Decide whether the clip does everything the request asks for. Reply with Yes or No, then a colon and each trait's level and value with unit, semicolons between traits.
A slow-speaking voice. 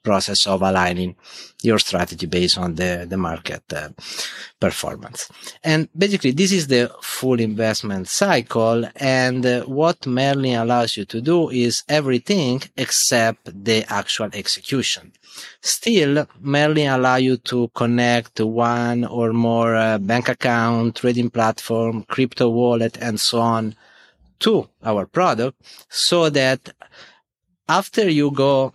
Yes: slow, 125 wpm